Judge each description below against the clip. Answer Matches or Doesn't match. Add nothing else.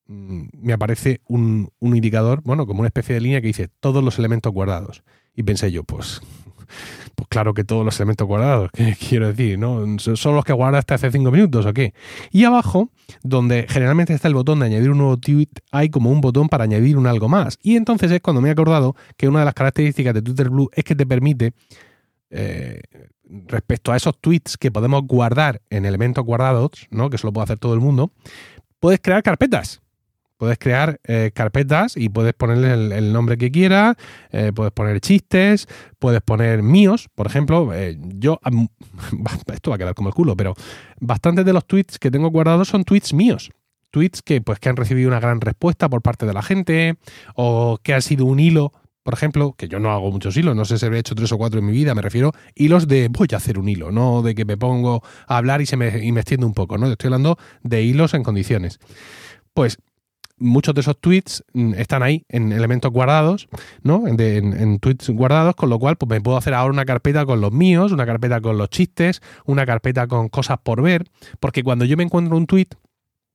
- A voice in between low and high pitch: Doesn't match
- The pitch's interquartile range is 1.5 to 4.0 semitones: Doesn't match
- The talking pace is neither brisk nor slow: Doesn't match